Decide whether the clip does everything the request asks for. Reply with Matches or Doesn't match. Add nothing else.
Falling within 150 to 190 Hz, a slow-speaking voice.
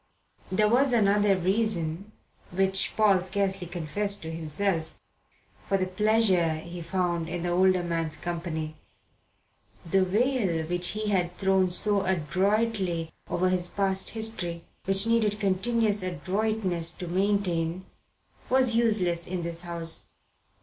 Matches